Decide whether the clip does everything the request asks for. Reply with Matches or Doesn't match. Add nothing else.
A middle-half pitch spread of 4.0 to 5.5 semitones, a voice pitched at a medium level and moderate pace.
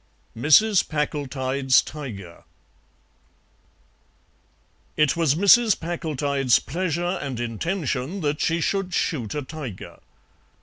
Doesn't match